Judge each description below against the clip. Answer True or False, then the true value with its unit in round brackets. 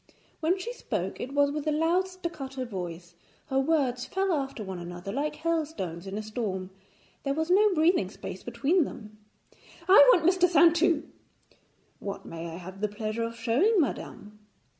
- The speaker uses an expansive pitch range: True (8.2 semitones)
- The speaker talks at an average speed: True (165 wpm)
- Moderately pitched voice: False (270 Hz)